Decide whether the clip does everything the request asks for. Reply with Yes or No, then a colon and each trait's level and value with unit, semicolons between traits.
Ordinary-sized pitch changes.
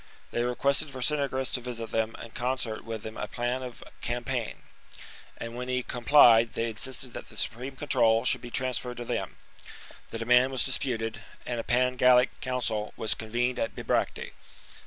No: narrow, 1.9 semitones